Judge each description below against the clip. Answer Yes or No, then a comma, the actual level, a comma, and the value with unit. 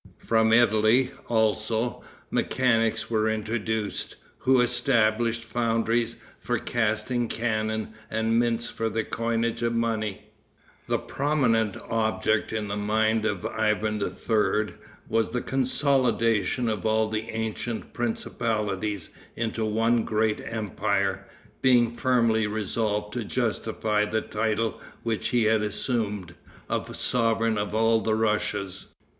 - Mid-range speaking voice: No, low, 110 Hz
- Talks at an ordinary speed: No, slow, 115 wpm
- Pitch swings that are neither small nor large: No, narrow, 1.4 semitones